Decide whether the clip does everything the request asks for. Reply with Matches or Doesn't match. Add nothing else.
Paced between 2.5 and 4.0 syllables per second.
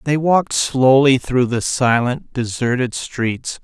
Matches